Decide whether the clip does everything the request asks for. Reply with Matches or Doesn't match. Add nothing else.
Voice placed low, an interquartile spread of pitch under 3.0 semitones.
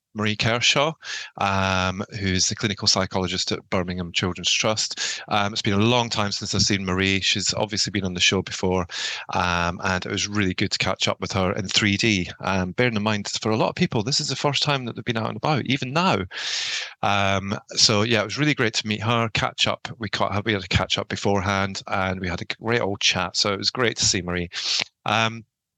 Doesn't match